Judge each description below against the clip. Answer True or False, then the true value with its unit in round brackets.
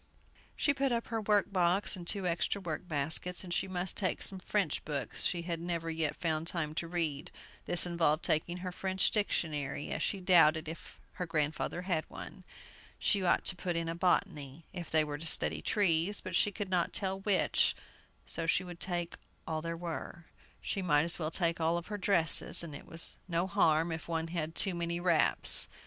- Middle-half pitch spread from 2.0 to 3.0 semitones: True (2.5 semitones)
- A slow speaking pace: False (195 wpm)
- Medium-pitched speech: True (170 Hz)